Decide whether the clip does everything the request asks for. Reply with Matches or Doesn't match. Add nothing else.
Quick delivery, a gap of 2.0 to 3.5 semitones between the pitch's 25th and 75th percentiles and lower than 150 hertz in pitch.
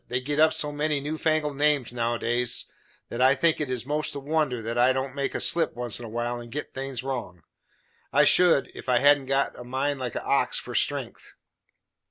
Matches